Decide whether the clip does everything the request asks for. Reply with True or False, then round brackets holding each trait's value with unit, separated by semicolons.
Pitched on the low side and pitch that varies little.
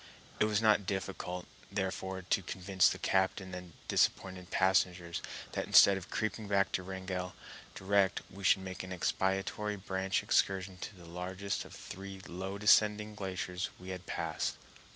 True (95 Hz; 1.2 semitones)